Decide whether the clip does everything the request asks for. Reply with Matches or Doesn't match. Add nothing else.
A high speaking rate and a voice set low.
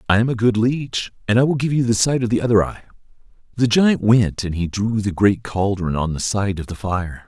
Matches